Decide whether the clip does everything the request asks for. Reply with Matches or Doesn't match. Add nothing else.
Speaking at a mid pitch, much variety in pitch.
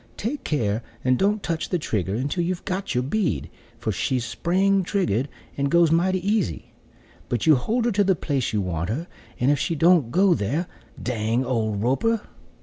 Matches